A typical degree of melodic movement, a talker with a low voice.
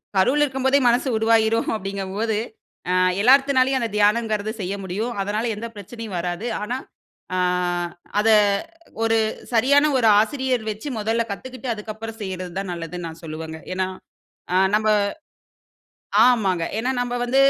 No: average, 4.0 semitones; high, 220 Hz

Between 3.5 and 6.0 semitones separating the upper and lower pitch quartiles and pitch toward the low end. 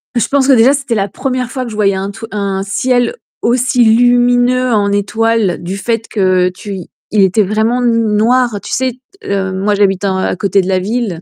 No: average, 3.8 semitones; high, 220 Hz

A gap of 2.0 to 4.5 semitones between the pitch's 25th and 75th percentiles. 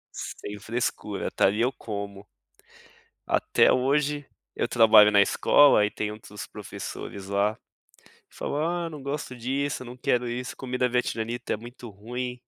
Yes: average, 3.4 semitones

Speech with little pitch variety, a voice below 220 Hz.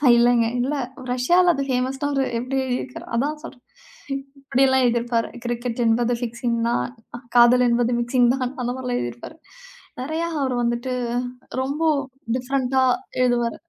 No: narrow, 2.0 semitones; very high, 250 Hz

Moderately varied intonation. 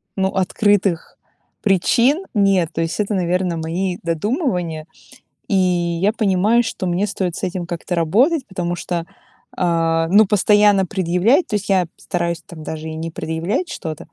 Yes: average, 3.4 semitones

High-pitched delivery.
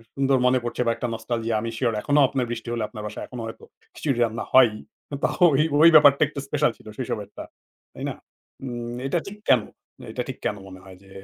No: low, 120 Hz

